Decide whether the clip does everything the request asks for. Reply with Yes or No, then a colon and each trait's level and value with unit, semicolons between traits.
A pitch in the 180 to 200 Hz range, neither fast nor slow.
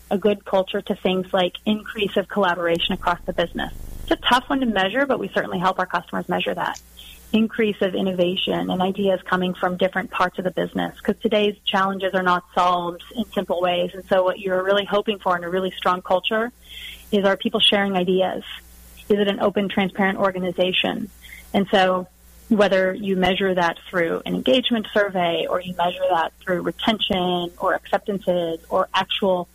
Yes: high, 190 Hz; average, 185 wpm